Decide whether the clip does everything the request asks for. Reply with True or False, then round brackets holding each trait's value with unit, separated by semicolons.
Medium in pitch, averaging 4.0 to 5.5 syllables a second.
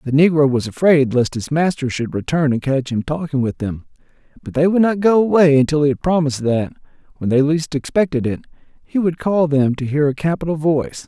False (145 Hz; 5.7 syllables/s)